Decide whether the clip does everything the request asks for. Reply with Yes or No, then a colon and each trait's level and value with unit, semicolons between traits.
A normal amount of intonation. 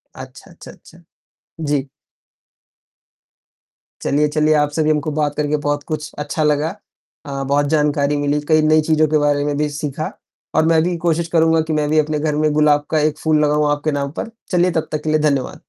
No: narrow, 1.2 semitones